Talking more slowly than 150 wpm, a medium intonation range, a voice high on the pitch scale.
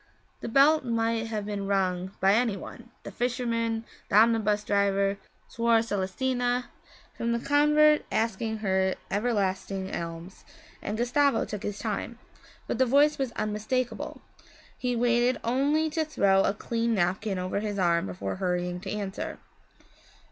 Yes: average, 140 wpm; average, 3.8 semitones; high, 220 Hz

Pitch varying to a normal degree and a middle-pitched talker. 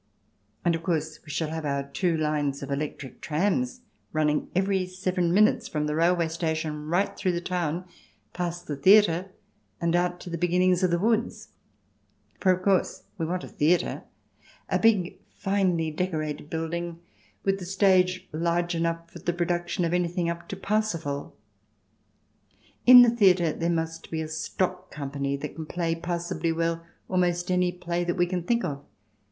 No: narrow, 2.3 semitones; medium, 175 Hz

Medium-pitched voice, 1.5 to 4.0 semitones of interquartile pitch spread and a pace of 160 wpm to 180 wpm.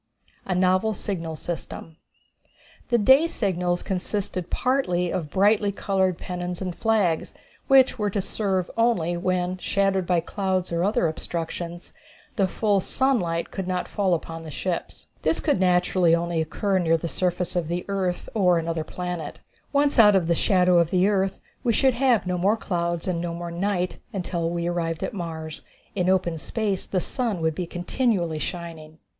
Yes: medium, 180 Hz; average, 2.8 semitones; average, 170 wpm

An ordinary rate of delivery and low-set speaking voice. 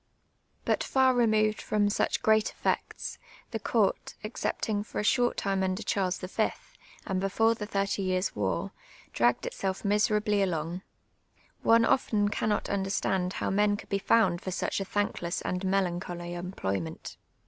No: average, 155 wpm; high, 195 Hz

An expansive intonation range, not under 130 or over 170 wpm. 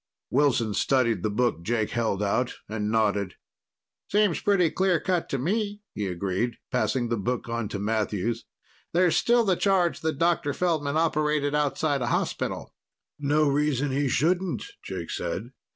Yes: wide, 7.0 semitones; average, 150 wpm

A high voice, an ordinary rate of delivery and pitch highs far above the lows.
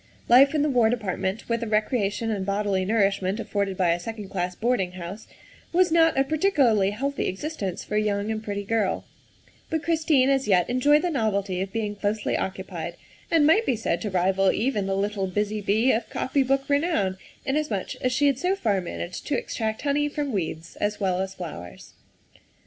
Yes: high, 215 Hz; average, 190 wpm; wide, 5.8 semitones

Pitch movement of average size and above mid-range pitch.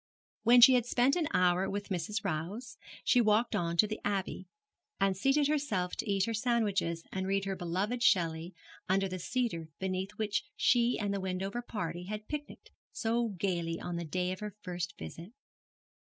Yes: average, 4.2 semitones; high, 195 Hz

